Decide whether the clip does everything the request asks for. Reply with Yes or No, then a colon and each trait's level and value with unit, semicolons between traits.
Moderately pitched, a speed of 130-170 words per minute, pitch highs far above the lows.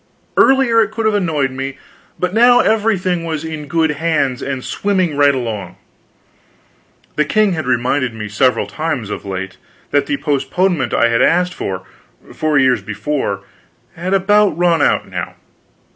Yes: medium, 155 Hz; average, 155 wpm; wide, 6.3 semitones